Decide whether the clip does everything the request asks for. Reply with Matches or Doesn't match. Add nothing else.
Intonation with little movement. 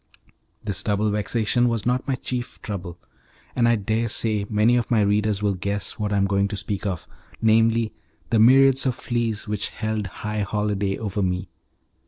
Matches